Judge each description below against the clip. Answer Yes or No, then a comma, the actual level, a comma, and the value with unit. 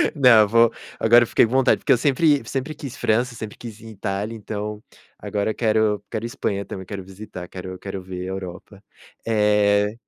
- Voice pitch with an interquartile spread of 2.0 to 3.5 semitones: Yes, average, 2.8 semitones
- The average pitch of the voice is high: No, low, 105 Hz